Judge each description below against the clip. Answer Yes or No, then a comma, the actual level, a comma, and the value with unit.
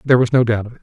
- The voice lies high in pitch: No, low, 120 Hz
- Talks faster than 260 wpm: Yes, fast, 440 wpm